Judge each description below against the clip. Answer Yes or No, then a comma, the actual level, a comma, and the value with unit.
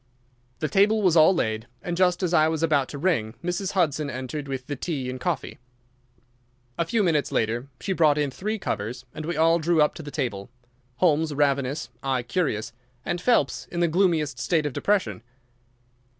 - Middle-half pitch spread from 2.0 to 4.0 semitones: No, average, 4.8 semitones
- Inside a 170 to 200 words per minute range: Yes, average, 185 wpm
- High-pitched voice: No, medium, 155 Hz